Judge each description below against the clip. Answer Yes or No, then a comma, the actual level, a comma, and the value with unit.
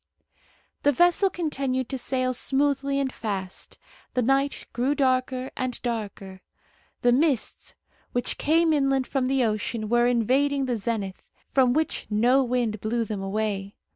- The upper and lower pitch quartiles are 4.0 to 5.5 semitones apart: No, average, 3.5 semitones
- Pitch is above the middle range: Yes, very high, 255 Hz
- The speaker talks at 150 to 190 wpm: No, average, 140 wpm